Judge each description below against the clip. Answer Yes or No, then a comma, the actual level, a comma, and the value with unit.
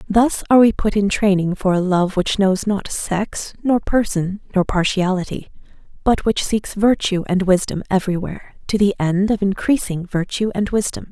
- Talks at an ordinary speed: Yes, average, 175 wpm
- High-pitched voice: Yes, high, 195 Hz